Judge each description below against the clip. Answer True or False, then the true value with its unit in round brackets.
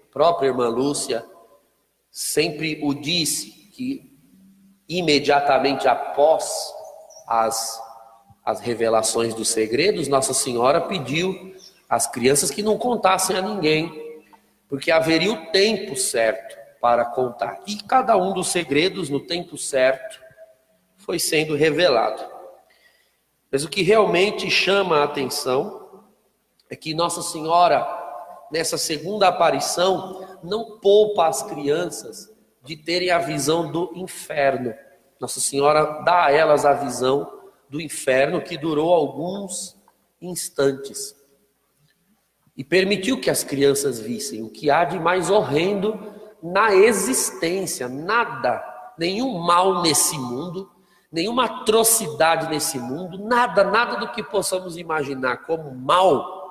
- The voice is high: False (170 Hz)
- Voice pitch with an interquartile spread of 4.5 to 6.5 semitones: True (5.5 semitones)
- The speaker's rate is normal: False (115 wpm)